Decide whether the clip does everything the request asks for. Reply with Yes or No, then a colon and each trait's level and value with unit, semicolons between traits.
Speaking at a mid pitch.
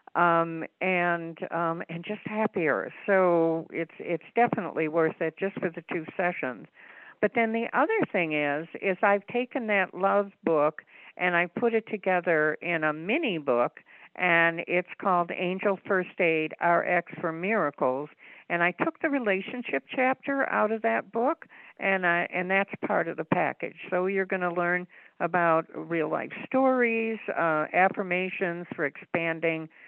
Yes: medium, 180 Hz